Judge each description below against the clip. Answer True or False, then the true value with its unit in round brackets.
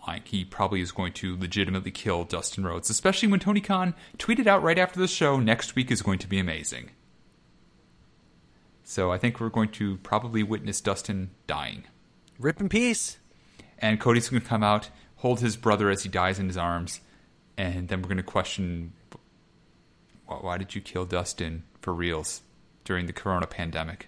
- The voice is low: True (95 Hz)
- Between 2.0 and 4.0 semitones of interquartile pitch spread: False (4.4 semitones)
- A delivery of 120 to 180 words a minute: True (175 wpm)